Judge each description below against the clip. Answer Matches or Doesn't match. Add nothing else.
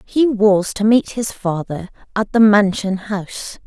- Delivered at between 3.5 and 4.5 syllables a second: Matches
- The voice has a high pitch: Matches